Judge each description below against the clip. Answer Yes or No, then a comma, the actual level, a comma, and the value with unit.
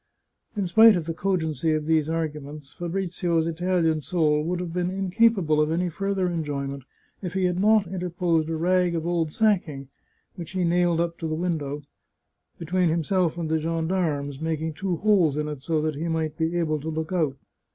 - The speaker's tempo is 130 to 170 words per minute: No, average, 190 wpm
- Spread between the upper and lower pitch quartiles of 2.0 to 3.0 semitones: Yes, narrow, 2.5 semitones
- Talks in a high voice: No, medium, 165 Hz